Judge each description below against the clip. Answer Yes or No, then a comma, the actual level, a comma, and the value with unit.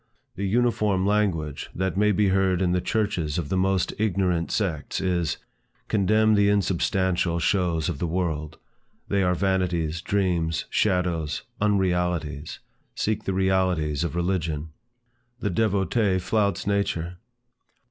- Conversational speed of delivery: No, slow, 125 wpm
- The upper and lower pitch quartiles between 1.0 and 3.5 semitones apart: Yes, average, 2.9 semitones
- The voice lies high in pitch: No, very low, 95 Hz